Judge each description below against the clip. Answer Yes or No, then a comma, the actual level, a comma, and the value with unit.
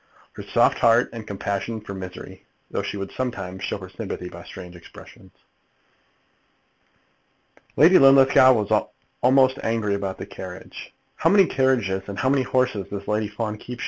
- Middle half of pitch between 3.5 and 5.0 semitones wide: Yes, average, 4.7 semitones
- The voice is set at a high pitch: No, low, 110 Hz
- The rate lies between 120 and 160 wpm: Yes, average, 155 wpm